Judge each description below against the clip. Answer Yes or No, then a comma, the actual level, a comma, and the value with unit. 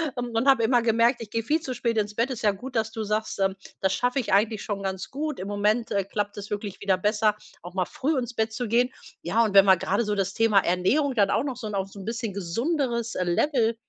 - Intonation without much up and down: No, average, 3.3 semitones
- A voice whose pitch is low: No, high, 220 Hz